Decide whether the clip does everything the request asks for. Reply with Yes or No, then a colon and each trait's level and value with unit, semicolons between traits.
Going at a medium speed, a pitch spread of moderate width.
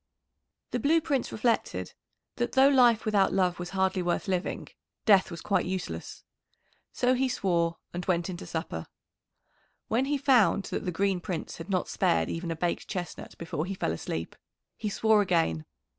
Yes: average, 175 wpm; average, 4.5 semitones